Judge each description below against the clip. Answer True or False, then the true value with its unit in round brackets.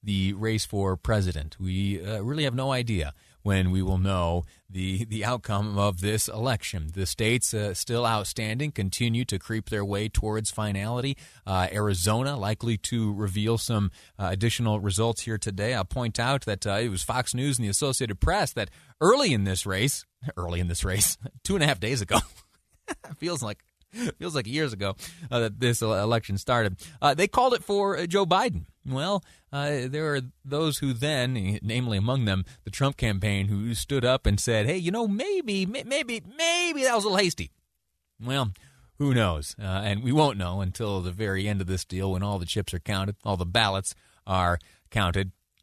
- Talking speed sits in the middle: True (190 wpm)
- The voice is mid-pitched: False (110 Hz)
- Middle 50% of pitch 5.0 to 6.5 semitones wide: True (5.4 semitones)